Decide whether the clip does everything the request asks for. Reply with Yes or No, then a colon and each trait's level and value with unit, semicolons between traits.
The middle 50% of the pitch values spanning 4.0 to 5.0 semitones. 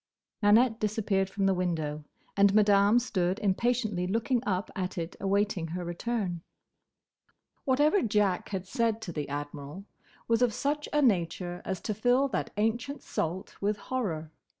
Yes: average, 4.3 semitones